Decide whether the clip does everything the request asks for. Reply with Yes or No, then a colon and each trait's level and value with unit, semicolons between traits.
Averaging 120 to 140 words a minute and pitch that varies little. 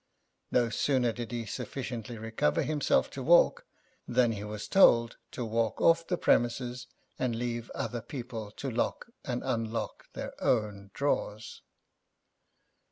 Yes: slow, 135 wpm; narrow, 2.2 semitones